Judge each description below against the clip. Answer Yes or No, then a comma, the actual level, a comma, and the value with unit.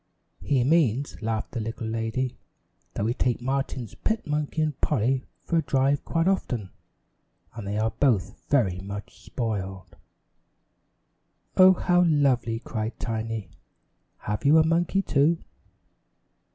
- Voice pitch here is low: Yes, low, 125 Hz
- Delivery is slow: Yes, slow, 130 wpm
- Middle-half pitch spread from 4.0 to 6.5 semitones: Yes, average, 5.2 semitones